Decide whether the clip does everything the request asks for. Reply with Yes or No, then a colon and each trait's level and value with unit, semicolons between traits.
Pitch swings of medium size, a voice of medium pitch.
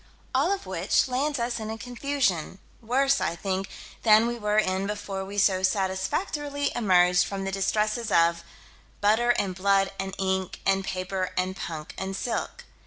No: average, 3.9 semitones; high, 195 Hz